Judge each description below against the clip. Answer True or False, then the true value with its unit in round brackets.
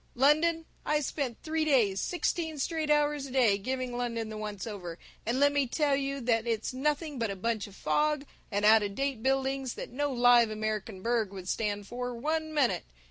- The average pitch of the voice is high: True (250 Hz)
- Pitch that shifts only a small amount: False (5.0 semitones)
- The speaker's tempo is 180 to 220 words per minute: True (195 wpm)